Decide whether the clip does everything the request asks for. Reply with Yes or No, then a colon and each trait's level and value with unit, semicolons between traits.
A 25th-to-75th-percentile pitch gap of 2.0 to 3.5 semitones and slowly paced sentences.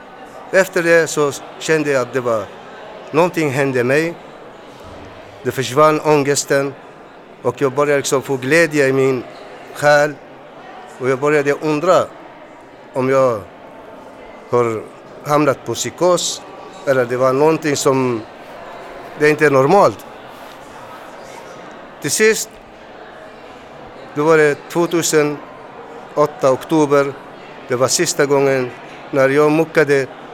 Yes: narrow, 2.6 semitones; slow, 110 wpm